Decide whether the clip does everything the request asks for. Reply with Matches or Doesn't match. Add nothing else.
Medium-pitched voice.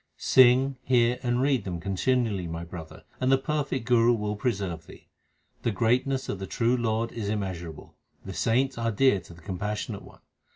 Doesn't match